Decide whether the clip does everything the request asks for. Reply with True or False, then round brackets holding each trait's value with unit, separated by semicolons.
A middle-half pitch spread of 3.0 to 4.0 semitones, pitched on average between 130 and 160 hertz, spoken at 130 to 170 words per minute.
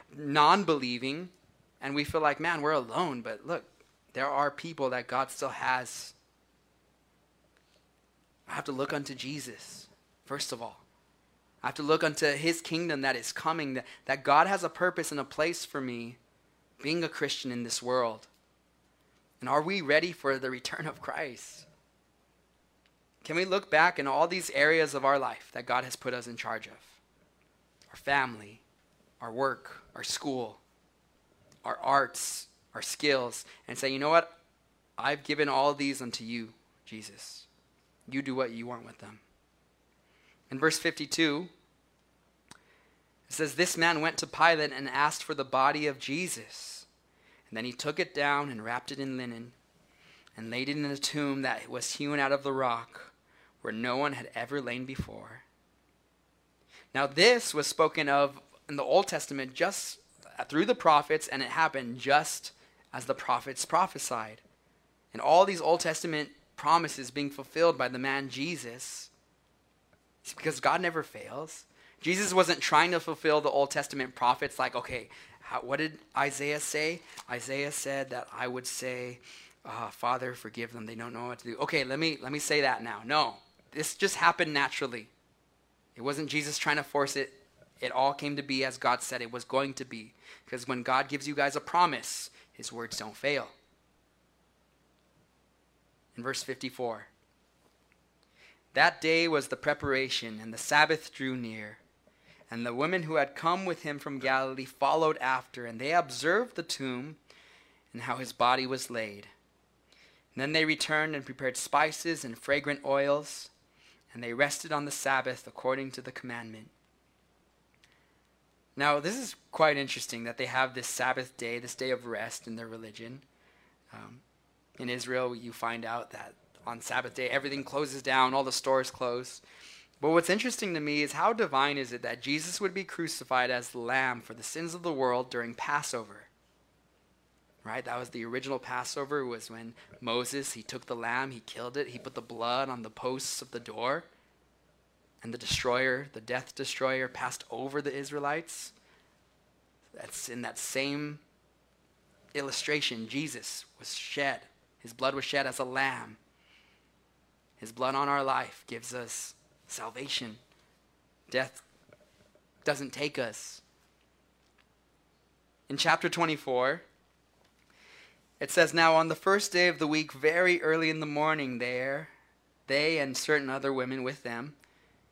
True (3.5 semitones; 135 Hz; 165 wpm)